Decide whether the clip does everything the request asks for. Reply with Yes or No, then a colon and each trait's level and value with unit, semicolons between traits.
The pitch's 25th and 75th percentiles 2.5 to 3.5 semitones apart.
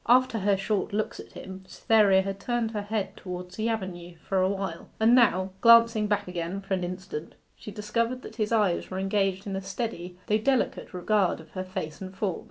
Yes: average, 2.8 semitones